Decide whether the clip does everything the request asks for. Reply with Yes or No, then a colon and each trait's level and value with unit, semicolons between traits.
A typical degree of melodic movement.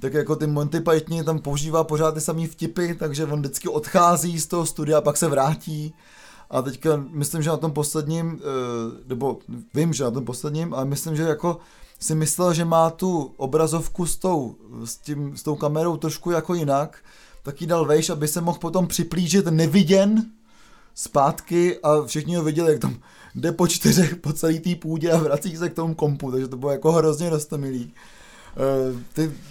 No: narrow, 2.3 semitones